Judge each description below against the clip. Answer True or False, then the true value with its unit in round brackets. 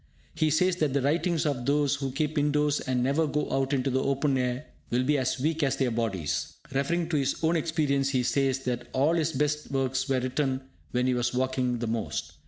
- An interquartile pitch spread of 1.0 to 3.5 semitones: True (2.7 semitones)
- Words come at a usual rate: False (215 wpm)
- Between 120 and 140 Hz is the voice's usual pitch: True (135 Hz)